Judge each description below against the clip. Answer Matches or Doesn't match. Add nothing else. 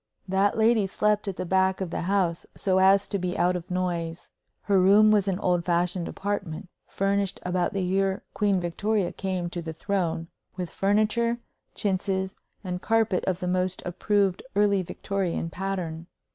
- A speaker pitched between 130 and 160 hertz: Doesn't match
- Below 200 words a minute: Matches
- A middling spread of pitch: Doesn't match